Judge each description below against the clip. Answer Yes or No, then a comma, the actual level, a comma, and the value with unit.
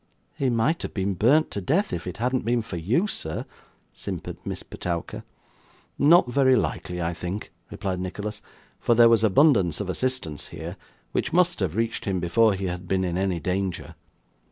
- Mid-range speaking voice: No, low, 100 Hz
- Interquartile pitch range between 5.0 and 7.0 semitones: Yes, wide, 5.6 semitones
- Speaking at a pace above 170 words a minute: Yes, average, 180 wpm